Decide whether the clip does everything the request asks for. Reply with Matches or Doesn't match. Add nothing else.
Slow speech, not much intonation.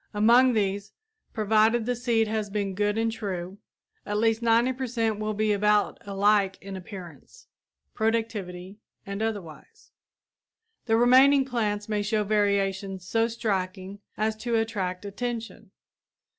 Matches